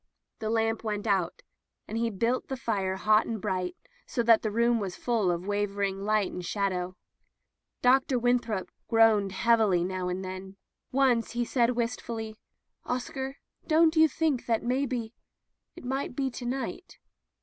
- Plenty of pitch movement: No, average, 3.8 semitones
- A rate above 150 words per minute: Yes, average, 160 wpm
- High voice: Yes, high, 225 Hz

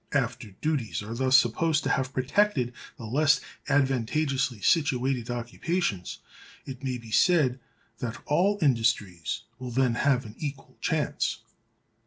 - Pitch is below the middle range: Yes, low, 130 Hz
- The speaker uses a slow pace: Yes, slow, 130 wpm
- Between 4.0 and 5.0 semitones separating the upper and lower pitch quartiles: No, average, 3.5 semitones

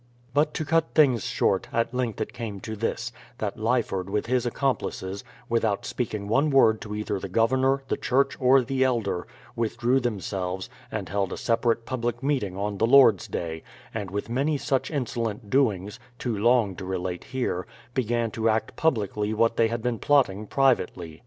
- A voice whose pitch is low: Yes, low, 115 Hz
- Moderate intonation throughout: Yes, average, 4.0 semitones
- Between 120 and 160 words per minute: No, average, 175 wpm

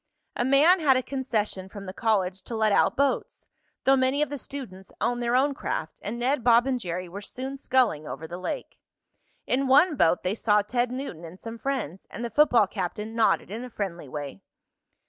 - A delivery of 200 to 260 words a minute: Yes, fast, 205 wpm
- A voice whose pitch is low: No, high, 230 Hz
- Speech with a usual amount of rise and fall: No, wide, 5.7 semitones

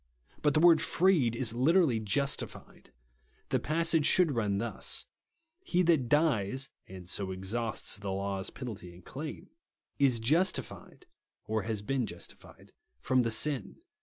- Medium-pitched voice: No, low, 125 Hz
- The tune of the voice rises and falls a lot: Yes, wide, 7.1 semitones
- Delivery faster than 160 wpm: No, average, 140 wpm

